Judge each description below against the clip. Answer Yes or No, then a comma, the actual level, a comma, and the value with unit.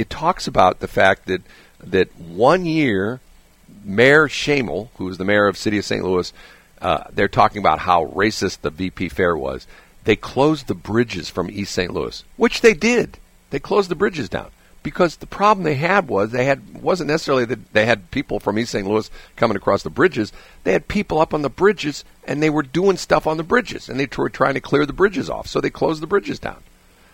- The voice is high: No, medium, 140 Hz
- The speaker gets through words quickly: Yes, fast, 220 wpm